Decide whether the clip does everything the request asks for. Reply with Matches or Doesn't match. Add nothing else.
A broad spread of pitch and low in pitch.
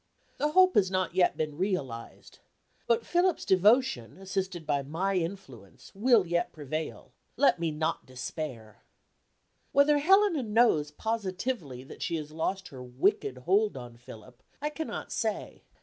Doesn't match